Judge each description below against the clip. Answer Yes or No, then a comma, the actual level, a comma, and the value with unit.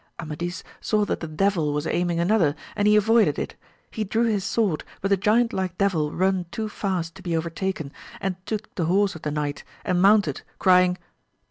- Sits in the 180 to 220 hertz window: Yes, medium, 185 Hz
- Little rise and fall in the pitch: No, average, 3.7 semitones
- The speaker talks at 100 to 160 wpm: No, average, 195 wpm